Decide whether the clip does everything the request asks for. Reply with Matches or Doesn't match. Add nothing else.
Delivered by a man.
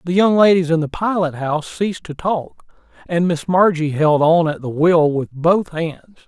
Matches